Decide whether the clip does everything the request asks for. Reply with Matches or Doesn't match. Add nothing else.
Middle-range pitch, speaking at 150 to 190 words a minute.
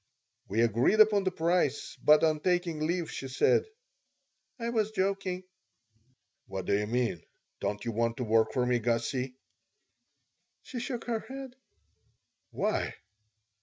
Doesn't match